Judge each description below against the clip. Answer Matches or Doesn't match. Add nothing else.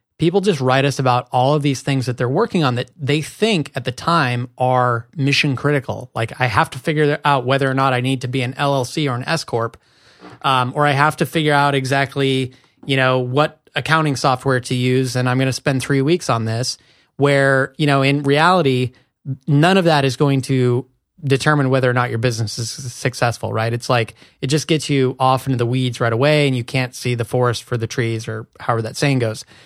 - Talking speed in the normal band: Doesn't match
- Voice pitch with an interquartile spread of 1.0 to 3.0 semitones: Matches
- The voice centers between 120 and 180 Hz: Matches